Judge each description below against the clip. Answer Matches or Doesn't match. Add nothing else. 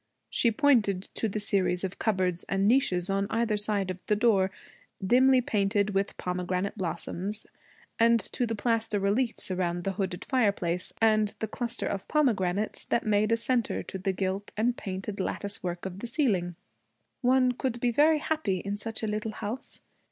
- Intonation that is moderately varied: Matches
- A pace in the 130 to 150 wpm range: Doesn't match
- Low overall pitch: Doesn't match